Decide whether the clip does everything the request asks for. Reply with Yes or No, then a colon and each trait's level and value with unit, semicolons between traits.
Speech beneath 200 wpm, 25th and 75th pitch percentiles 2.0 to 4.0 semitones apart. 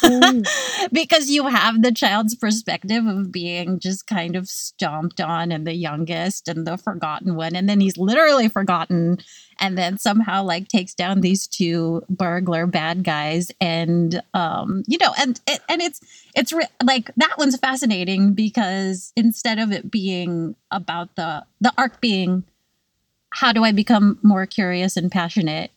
No: average, 160 wpm; average, 4.6 semitones